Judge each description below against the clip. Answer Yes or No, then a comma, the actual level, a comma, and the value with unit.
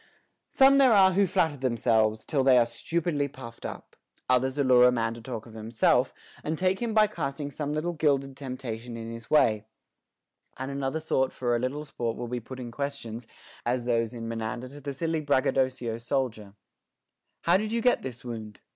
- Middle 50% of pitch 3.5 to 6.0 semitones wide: Yes, average, 4.2 semitones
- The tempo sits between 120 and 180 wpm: No, average, 190 wpm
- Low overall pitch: Yes, low, 130 Hz